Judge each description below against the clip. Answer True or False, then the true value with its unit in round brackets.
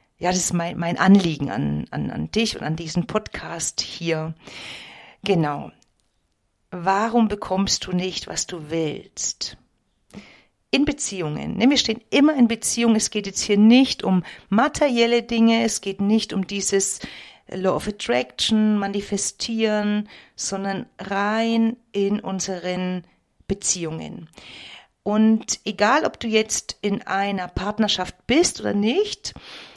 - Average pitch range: True (3.4 semitones)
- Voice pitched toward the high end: True (200 Hz)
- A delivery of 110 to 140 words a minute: True (125 wpm)